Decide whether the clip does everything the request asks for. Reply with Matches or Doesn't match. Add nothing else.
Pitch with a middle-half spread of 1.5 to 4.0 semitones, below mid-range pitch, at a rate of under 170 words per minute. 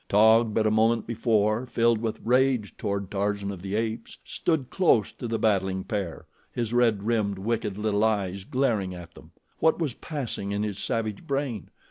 Doesn't match